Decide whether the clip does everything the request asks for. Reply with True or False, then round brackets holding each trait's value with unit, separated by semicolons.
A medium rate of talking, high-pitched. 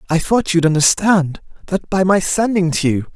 False (190 wpm; 175 Hz)